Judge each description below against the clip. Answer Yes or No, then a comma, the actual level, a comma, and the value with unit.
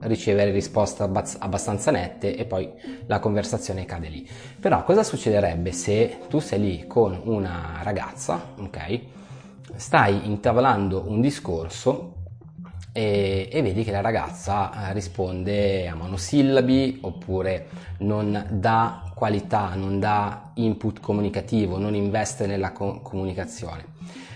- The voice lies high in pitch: No, low, 100 Hz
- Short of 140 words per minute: Yes, average, 120 wpm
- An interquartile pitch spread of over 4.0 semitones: No, average, 3.3 semitones